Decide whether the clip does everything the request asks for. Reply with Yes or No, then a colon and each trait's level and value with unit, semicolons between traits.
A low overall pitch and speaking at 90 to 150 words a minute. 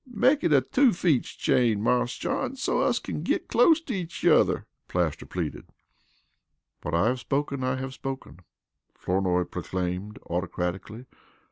Yes: low, 125 Hz; average, 145 wpm